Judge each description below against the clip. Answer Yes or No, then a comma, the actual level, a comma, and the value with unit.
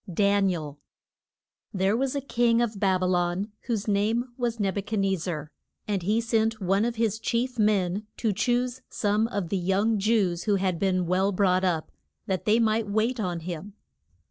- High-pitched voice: Yes, high, 205 Hz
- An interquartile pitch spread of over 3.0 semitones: Yes, average, 3.4 semitones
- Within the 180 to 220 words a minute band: Yes, average, 185 wpm